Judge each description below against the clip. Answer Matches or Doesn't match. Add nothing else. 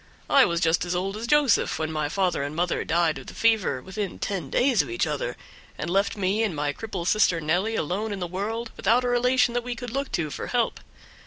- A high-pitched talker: Matches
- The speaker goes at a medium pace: Doesn't match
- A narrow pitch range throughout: Doesn't match